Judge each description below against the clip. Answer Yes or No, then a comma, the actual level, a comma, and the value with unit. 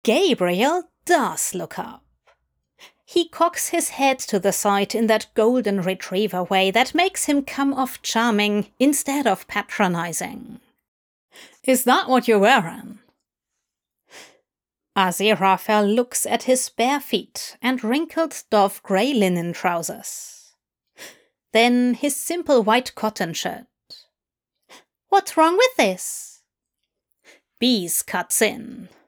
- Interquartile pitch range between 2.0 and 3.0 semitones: No, average, 5.1 semitones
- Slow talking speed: Yes, slow, 115 wpm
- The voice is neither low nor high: No, high, 235 Hz